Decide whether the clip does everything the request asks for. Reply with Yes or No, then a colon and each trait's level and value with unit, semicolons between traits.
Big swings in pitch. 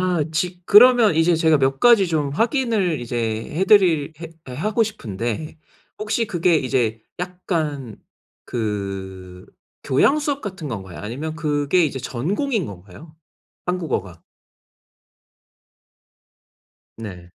Yes: wide, 7.9 semitones